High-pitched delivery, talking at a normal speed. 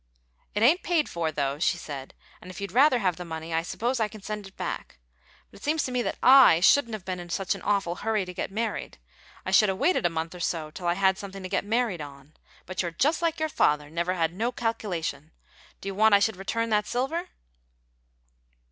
No: high, 195 Hz; fast, 230 wpm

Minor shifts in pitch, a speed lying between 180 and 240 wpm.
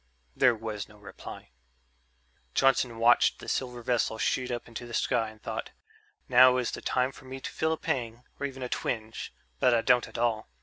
Yes: narrow, 2.1 semitones; average, 200 wpm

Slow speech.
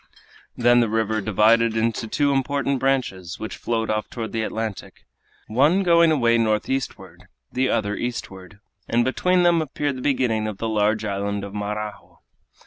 No: average, 155 wpm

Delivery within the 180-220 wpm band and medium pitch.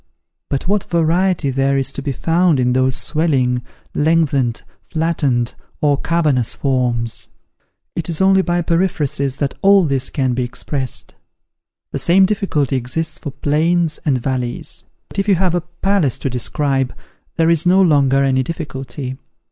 No: average, 150 wpm; medium, 145 Hz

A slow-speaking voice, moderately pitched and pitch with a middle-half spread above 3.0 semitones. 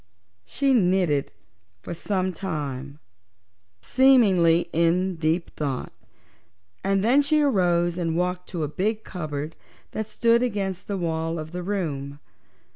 Yes: slow, 125 wpm; medium, 180 Hz; average, 3.8 semitones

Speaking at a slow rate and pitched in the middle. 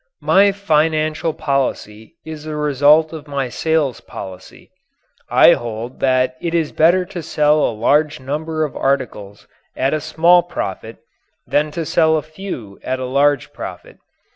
No: average, 150 wpm; medium, 150 Hz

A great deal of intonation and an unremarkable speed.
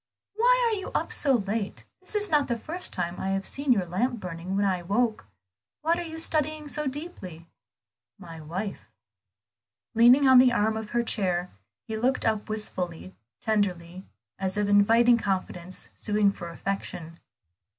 Yes: wide, 6.1 semitones; average, 160 wpm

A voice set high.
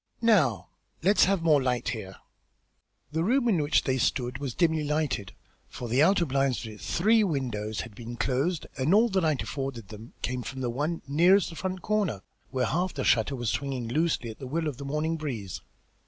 No: medium, 140 Hz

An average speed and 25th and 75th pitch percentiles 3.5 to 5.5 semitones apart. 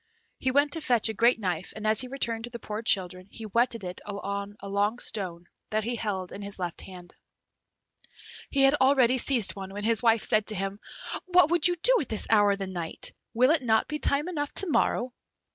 No: fast, 225 wpm; average, 4.6 semitones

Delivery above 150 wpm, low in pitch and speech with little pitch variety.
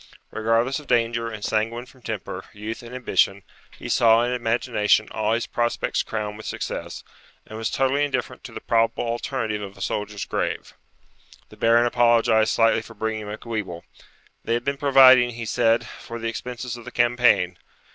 Yes: average, 170 wpm; low, 115 Hz; narrow, 1.9 semitones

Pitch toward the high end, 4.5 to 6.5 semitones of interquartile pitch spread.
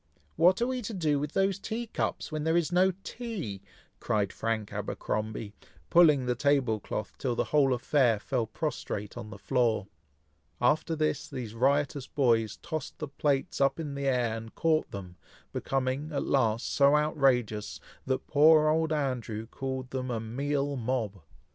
No: low, 135 Hz; average, 5.1 semitones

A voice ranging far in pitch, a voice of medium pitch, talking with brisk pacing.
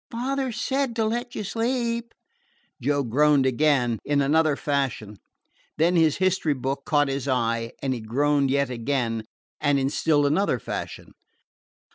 No: wide, 6.2 semitones; medium, 145 Hz; average, 145 wpm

